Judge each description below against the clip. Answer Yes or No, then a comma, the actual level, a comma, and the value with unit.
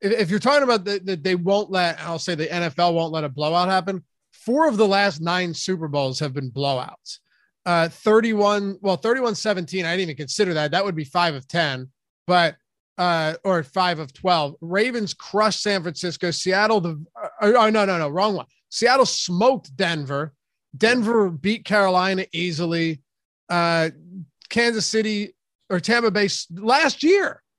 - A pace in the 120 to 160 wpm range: No, average, 170 wpm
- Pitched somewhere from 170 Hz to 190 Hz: Yes, medium, 185 Hz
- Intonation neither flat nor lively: Yes, average, 4.1 semitones